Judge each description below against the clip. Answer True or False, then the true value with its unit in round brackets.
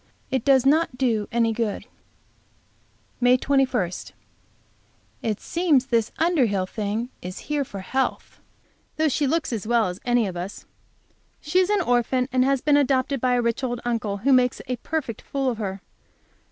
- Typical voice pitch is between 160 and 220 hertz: False (250 Hz)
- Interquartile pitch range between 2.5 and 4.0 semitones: True (3.6 semitones)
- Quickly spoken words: False (165 wpm)